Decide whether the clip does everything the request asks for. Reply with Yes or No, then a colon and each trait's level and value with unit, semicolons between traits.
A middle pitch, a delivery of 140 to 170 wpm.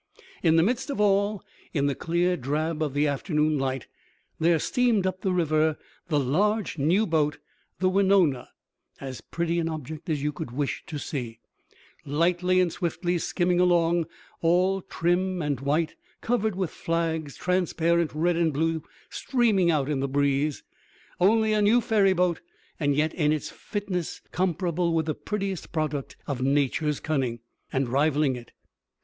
Yes: medium, 165 Hz; average, 155 wpm